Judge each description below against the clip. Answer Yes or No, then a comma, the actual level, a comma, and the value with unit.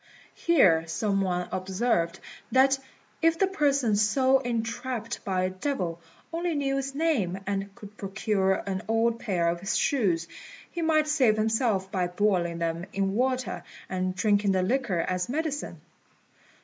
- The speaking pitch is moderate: No, high, 210 Hz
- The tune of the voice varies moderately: No, wide, 6.2 semitones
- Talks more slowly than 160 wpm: Yes, average, 150 wpm